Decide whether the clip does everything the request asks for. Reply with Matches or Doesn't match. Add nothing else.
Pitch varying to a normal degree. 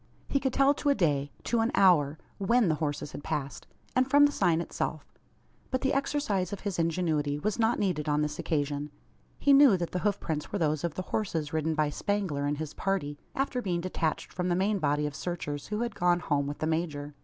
Doesn't match